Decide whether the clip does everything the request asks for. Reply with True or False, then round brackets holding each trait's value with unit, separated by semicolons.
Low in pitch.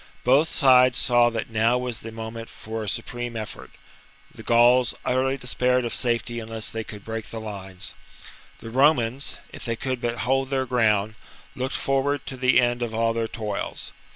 True (120 Hz)